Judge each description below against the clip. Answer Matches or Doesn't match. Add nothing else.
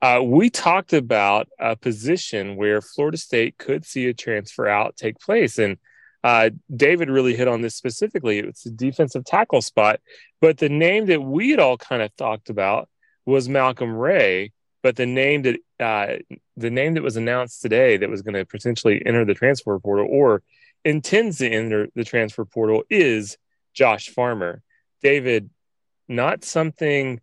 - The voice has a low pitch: Matches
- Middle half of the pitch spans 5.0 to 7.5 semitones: Matches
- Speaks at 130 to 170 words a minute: Matches